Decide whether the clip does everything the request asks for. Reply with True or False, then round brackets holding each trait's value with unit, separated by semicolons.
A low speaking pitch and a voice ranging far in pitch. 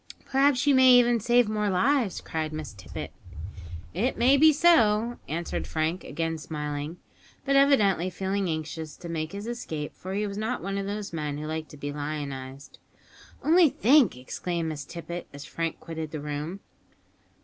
False (175 Hz; 7.2 semitones)